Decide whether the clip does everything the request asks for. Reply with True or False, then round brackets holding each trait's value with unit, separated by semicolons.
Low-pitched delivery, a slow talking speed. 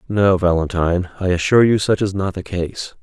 False (95 Hz; 200 wpm)